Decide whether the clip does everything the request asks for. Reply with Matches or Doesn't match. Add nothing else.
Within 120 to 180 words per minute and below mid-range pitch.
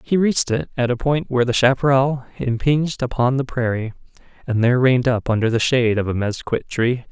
Doesn't match